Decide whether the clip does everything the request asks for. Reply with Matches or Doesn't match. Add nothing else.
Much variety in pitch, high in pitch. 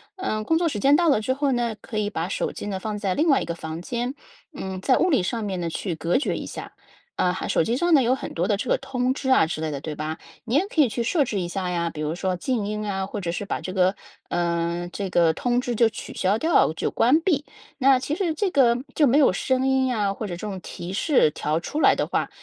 Matches